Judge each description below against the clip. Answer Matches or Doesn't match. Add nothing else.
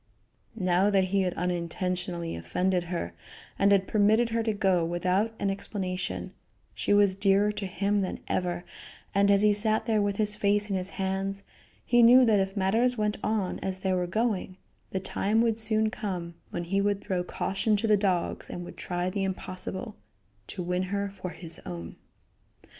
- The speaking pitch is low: Doesn't match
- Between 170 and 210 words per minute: Matches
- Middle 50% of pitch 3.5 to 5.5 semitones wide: Doesn't match